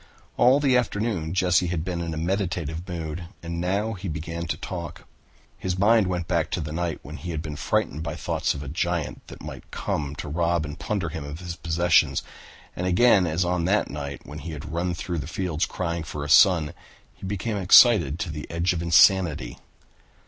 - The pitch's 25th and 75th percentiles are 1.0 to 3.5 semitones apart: Yes, average, 2.7 semitones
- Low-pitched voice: Yes, very low, 85 Hz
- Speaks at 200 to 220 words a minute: Yes, fast, 205 wpm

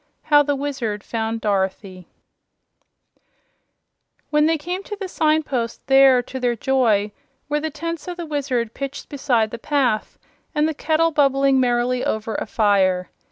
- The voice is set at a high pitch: Yes, very high, 270 Hz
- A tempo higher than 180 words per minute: No, average, 150 wpm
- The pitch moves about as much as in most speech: Yes, average, 4.9 semitones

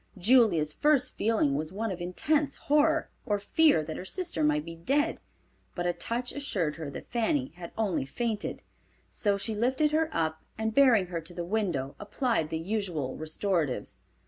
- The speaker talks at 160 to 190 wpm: Yes, average, 170 wpm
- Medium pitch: No, high, 205 Hz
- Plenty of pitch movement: Yes, wide, 7.5 semitones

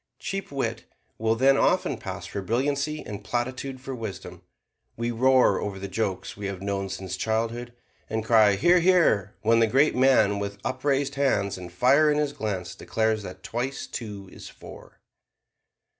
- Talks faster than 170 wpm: No, average, 165 wpm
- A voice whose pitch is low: Yes, low, 115 Hz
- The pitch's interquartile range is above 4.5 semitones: Yes, average, 5.1 semitones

